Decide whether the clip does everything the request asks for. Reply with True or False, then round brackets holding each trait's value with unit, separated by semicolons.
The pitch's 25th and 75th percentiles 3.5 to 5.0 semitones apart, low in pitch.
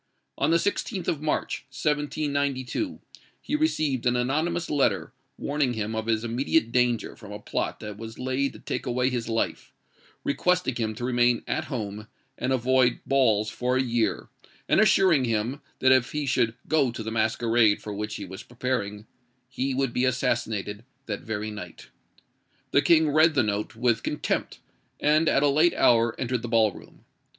True (4.1 semitones; 125 Hz)